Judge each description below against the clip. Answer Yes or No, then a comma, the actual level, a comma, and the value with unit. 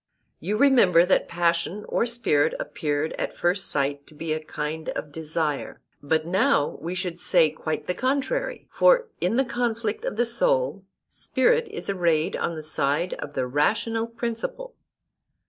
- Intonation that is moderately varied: No, wide, 7.2 semitones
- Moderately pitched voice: Yes, medium, 180 Hz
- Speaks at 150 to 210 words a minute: Yes, average, 160 wpm